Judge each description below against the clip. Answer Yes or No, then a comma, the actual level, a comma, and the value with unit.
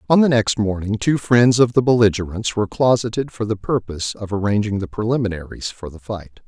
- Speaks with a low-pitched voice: Yes, low, 105 Hz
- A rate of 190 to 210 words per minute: Yes, fast, 205 wpm